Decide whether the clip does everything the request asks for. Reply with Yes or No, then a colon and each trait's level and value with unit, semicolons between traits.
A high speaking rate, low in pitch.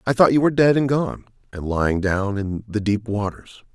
Yes: fast, 225 wpm; low, 110 Hz